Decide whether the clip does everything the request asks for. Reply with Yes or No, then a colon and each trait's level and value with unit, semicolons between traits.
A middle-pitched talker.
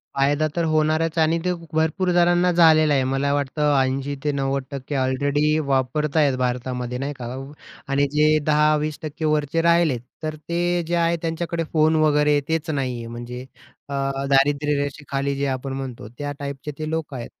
Yes: medium, 145 Hz